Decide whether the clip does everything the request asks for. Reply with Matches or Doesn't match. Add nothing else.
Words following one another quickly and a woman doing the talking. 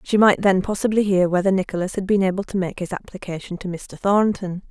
Matches